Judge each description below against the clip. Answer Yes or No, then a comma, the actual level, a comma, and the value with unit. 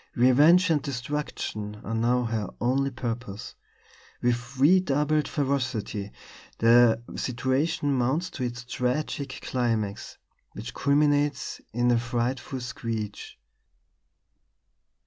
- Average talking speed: No, slow, 95 wpm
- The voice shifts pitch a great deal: No, average, 3.3 semitones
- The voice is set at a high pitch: No, low, 125 Hz